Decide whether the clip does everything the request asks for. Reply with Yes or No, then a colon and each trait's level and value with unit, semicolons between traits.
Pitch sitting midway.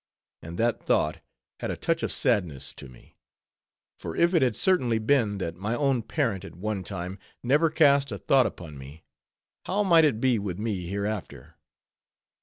No: low, 110 Hz